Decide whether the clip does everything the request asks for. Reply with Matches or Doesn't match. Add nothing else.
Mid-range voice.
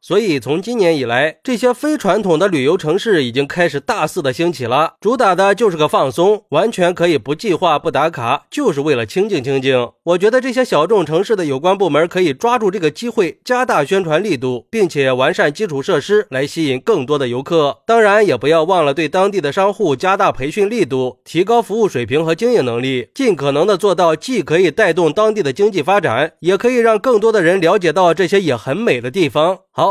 Matches